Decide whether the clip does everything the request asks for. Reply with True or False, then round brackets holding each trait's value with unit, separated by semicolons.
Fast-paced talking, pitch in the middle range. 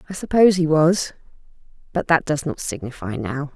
False (170 wpm; 155 Hz)